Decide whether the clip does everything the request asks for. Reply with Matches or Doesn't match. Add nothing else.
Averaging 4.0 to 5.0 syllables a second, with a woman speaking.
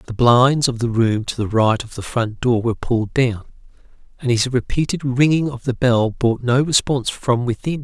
Doesn't match